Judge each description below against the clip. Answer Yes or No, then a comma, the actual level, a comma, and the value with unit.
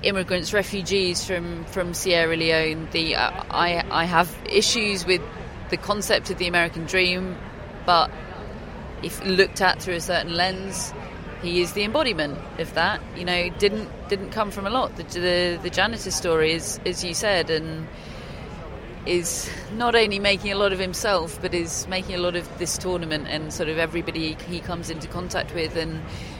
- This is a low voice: No, medium, 180 Hz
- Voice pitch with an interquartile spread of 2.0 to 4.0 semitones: Yes, narrow, 2.4 semitones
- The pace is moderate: Yes, average, 175 wpm